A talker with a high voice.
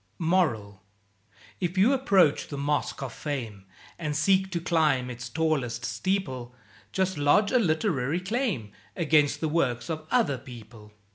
No: medium, 155 Hz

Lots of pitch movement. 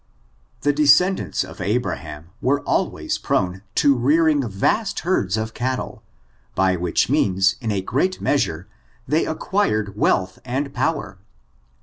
Yes: wide, 7.3 semitones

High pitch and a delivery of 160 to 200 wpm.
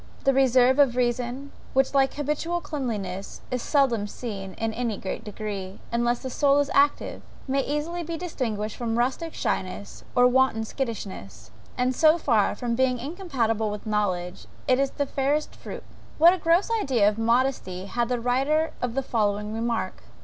Yes: high, 245 Hz; average, 165 wpm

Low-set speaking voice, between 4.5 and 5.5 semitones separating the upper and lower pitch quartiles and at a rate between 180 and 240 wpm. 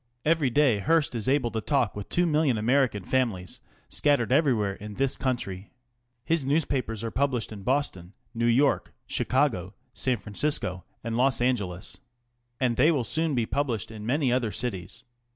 No: low, 125 Hz; average, 4.9 semitones; average, 160 wpm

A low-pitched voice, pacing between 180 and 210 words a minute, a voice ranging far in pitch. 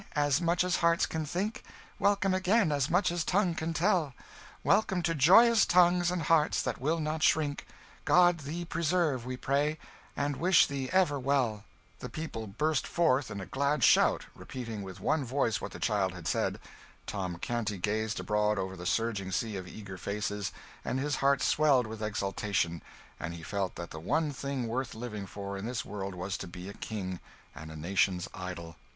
Yes: low, 130 Hz; average, 185 wpm; wide, 8.2 semitones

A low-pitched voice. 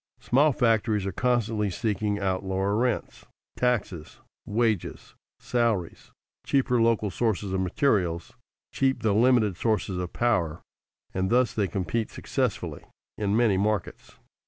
Yes: low, 105 Hz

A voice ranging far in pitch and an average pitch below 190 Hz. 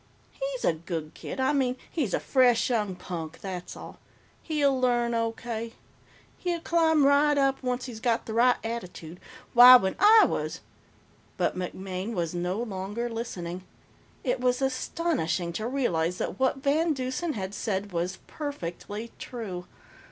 No: wide, 6.3 semitones; high, 235 Hz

